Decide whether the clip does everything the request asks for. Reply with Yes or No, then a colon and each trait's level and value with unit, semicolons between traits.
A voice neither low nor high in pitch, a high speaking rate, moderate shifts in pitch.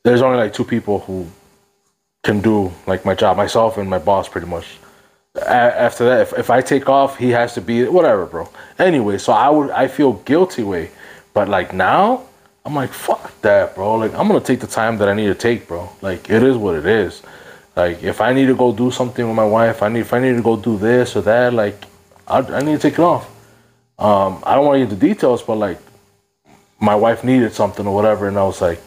No: low, 110 Hz; fast, 235 wpm; average, 3.5 semitones